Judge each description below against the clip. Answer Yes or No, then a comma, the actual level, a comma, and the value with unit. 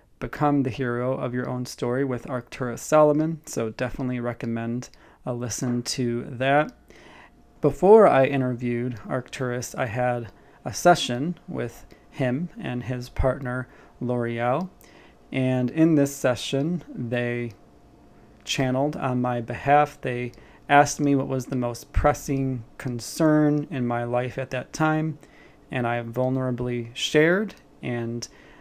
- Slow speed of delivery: Yes, slow, 125 wpm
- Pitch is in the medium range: No, low, 125 Hz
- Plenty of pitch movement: No, average, 2.9 semitones